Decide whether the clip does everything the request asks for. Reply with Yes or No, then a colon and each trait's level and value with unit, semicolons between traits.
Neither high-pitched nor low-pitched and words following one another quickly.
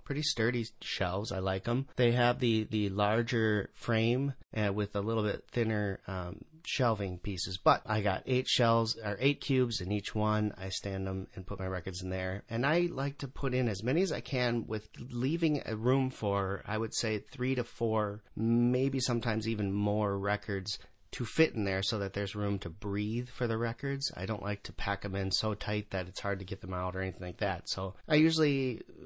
No: low, 110 Hz; fast, 215 wpm